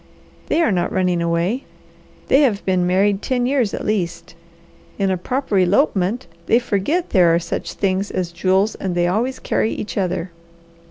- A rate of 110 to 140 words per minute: No, average, 170 wpm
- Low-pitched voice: No, high, 195 Hz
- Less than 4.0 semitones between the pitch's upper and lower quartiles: No, average, 4.5 semitones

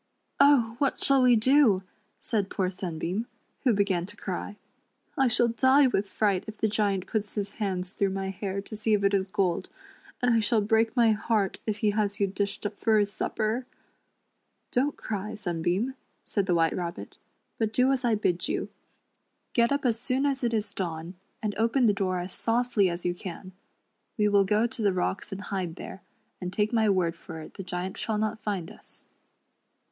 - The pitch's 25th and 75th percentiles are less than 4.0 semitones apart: Yes, average, 3.2 semitones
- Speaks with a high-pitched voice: Yes, high, 205 Hz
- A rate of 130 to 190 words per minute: No, fast, 205 wpm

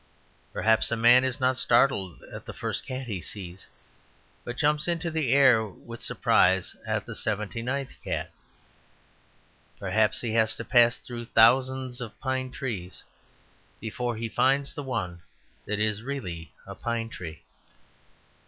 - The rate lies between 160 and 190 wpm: No, average, 145 wpm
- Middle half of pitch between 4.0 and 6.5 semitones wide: No, average, 3.5 semitones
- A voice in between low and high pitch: No, low, 120 Hz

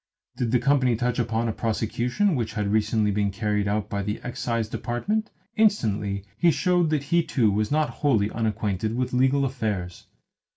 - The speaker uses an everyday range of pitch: Yes, average, 4.3 semitones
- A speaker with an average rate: Yes, average, 170 wpm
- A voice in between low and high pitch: No, low, 115 Hz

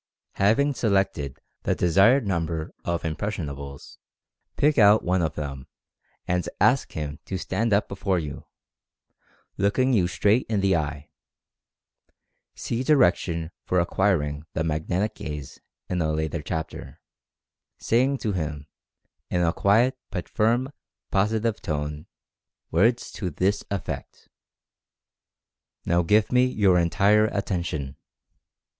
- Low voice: Yes, very low, 90 Hz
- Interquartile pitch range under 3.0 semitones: No, average, 5.3 semitones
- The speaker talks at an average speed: No, slow, 125 wpm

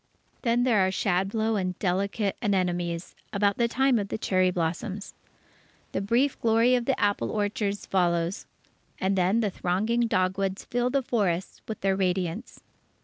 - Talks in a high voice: Yes, high, 200 Hz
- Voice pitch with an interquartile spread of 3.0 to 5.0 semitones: Yes, average, 3.7 semitones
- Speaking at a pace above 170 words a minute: No, average, 150 wpm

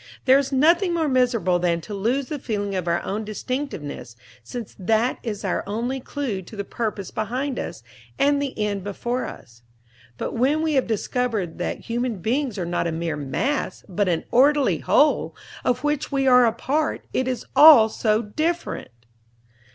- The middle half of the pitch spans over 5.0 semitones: Yes, wide, 5.4 semitones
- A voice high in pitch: Yes, high, 235 Hz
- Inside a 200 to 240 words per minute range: No, average, 175 wpm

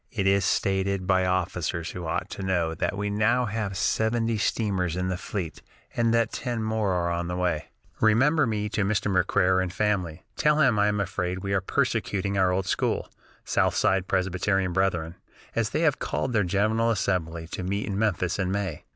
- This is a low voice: Yes, very low, 95 Hz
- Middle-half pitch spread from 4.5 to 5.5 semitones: No, average, 2.9 semitones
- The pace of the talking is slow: No, average, 190 wpm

